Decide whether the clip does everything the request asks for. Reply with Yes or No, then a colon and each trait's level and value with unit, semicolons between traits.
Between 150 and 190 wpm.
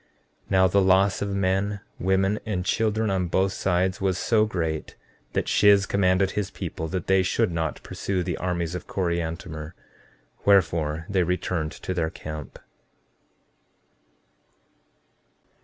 No: slow, 135 wpm